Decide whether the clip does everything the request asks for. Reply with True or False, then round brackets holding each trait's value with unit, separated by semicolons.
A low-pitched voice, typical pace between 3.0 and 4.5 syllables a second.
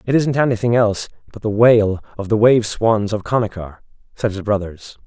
False (110 Hz; 5.3 syllables/s)